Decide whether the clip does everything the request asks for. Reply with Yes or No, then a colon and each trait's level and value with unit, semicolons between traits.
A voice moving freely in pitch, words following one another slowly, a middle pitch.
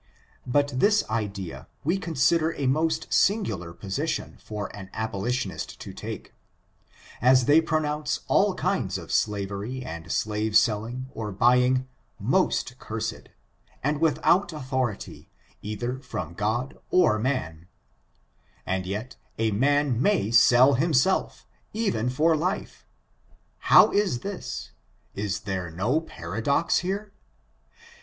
No: wide, 6.4 semitones; slow, 115 wpm; low, 125 Hz